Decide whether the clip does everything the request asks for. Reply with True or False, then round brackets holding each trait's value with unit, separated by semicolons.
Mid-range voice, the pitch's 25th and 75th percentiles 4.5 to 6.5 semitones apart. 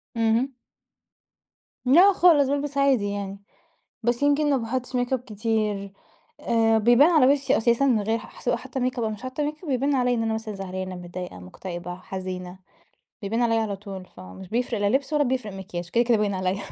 False (225 Hz; 4.9 semitones)